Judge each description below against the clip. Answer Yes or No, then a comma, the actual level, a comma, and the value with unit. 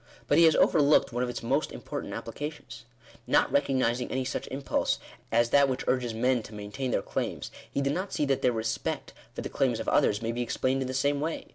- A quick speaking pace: Yes, fast, 225 wpm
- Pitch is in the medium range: No, low, 130 Hz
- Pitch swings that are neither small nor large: Yes, average, 3.0 semitones